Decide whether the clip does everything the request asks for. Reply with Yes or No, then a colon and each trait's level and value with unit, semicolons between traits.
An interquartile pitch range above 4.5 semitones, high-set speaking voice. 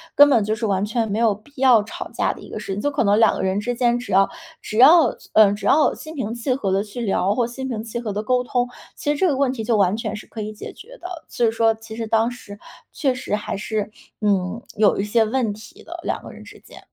No: average, 3.2 semitones; high, 225 Hz